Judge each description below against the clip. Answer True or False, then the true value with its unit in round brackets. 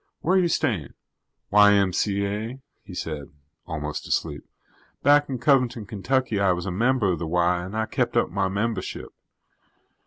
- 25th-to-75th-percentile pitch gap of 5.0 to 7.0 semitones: True (5.3 semitones)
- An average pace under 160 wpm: True (150 wpm)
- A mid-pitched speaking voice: False (100 Hz)